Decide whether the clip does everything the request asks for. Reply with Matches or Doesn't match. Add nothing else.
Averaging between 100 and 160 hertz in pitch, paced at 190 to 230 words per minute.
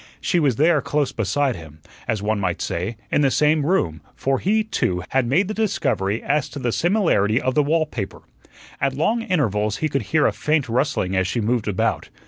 Matches